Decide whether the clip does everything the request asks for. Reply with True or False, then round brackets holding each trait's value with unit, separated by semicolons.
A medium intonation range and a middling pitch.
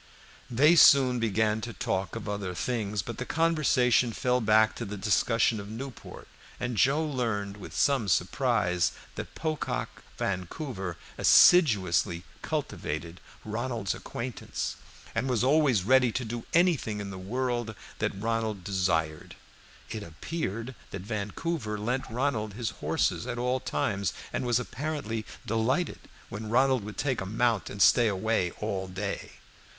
False (4.0 semitones; 115 Hz)